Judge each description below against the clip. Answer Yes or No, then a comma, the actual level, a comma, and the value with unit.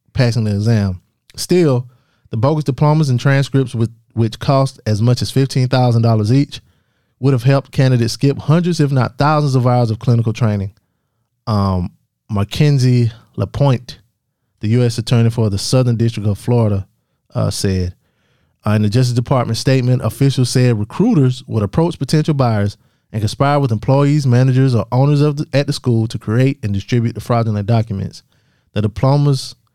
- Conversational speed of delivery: Yes, average, 155 wpm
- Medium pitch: No, low, 120 Hz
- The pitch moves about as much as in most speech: Yes, average, 3.5 semitones